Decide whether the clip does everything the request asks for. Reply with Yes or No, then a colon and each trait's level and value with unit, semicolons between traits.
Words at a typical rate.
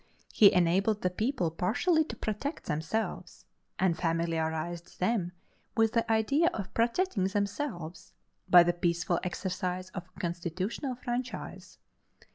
No: slow, 120 wpm